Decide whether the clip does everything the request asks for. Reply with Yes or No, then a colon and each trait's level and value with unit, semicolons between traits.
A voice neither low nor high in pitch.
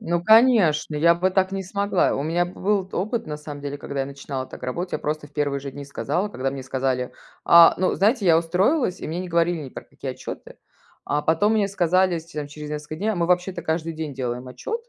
Yes: medium, 165 Hz